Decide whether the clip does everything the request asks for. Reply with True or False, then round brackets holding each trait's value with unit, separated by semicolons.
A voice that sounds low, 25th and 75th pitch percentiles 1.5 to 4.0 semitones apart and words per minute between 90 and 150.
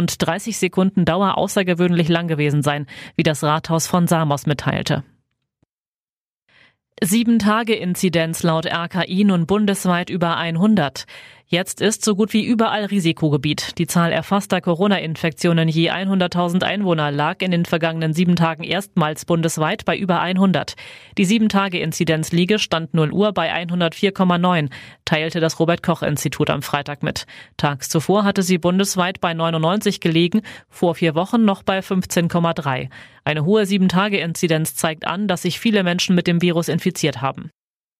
False (175 Hz; 2.9 semitones; 140 wpm)